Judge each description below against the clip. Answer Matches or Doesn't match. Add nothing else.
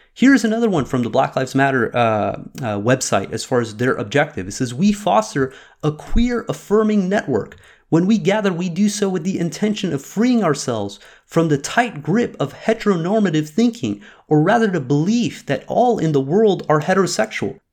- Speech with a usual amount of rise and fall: Doesn't match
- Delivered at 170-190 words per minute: Matches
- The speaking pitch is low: Doesn't match